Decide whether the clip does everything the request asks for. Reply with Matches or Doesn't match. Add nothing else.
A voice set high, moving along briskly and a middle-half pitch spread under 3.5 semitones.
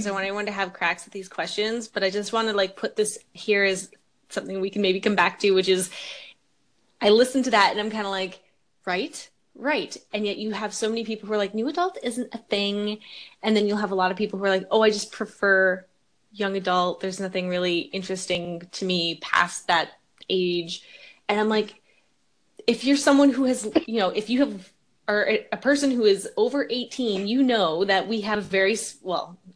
Matches